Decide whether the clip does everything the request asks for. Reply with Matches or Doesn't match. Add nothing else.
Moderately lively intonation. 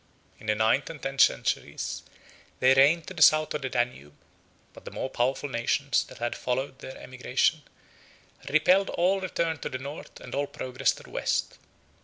Matches